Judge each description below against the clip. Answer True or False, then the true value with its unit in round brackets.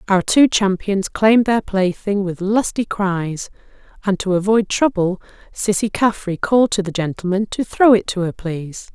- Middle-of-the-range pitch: False (200 Hz)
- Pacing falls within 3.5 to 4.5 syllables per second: False (4.7 syllables/s)